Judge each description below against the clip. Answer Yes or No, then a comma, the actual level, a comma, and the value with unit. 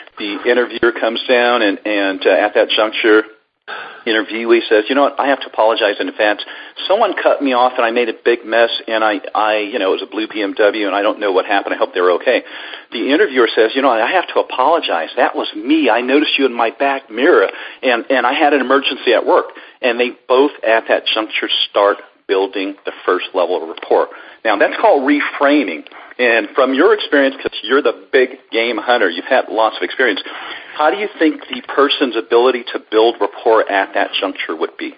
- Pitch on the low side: Yes, low, 125 Hz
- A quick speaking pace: Yes, fast, 215 wpm